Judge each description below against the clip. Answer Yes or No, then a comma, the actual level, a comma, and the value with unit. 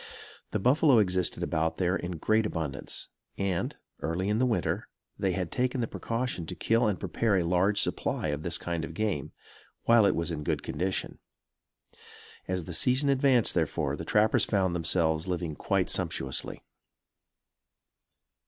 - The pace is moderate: Yes, average, 155 wpm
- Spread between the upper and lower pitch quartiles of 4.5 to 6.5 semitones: Yes, average, 5.0 semitones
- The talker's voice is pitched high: No, very low, 95 Hz